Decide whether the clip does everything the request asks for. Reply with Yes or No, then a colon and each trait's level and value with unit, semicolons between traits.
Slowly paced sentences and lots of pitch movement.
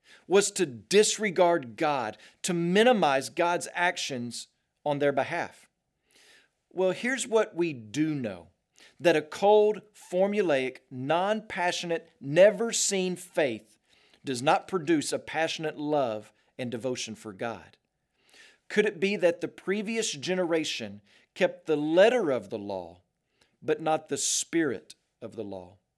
Yes: slow, 130 wpm; wide, 7.1 semitones